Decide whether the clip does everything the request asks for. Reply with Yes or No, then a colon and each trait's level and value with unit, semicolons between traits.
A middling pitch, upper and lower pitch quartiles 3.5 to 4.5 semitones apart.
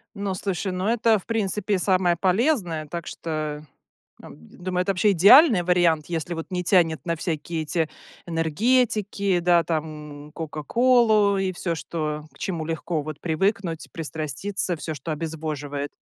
Yes: medium, 175 Hz; average, 3.9 semitones